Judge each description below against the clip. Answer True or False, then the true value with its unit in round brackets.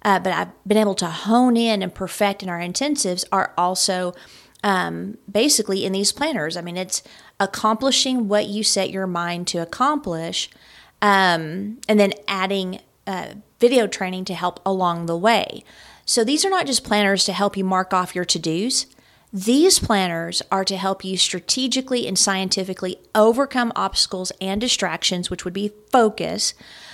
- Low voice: False (195 Hz)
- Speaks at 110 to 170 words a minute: True (165 wpm)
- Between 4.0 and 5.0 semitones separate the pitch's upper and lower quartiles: False (3.1 semitones)